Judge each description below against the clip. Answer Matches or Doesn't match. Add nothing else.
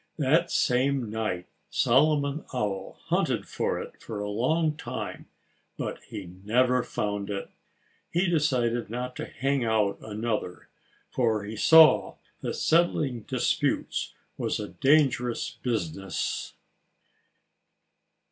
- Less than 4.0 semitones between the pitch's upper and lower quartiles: Doesn't match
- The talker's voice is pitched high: Doesn't match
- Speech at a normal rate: Doesn't match